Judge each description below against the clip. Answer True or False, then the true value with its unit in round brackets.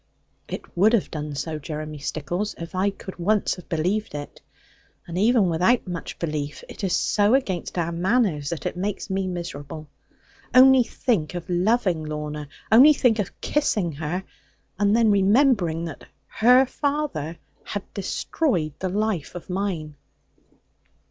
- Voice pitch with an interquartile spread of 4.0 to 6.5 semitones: True (5.2 semitones)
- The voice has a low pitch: False (185 Hz)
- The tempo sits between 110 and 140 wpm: False (150 wpm)